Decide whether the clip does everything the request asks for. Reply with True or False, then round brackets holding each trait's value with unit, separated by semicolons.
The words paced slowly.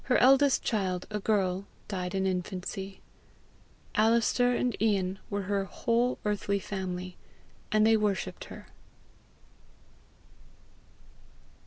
True (105 wpm)